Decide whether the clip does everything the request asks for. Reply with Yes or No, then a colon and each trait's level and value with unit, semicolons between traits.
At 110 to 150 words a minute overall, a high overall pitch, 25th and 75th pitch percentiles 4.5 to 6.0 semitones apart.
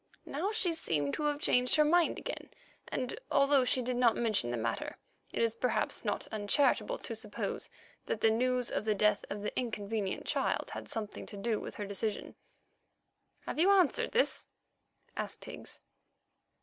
No: average, 170 wpm; high, 235 Hz; wide, 5.5 semitones